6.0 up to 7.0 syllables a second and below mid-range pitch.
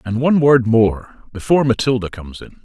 Yes: 6.1 syllables/s; low, 120 Hz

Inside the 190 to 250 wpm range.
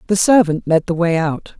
Yes: fast, 225 wpm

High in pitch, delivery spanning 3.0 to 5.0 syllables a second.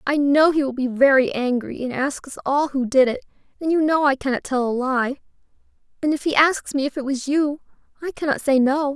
No: very high, 275 Hz; 5.5 syllables/s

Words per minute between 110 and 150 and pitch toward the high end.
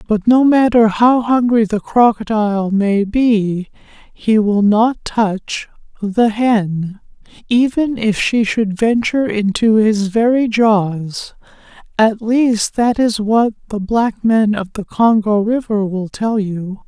Yes: average, 140 wpm; high, 215 Hz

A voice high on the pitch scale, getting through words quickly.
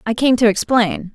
Yes: high, 225 Hz; fast, 210 wpm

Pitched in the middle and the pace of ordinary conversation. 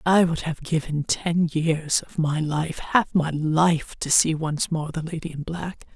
Yes: medium, 160 Hz; average, 180 wpm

